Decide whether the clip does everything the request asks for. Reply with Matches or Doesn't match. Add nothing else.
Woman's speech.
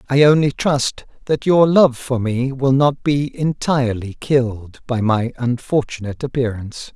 Doesn't match